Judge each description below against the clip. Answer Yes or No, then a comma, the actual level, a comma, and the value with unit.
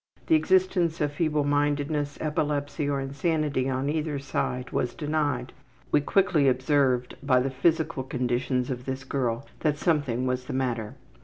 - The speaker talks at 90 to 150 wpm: Yes, average, 145 wpm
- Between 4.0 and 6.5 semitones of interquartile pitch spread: No, average, 2.8 semitones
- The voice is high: No, medium, 140 Hz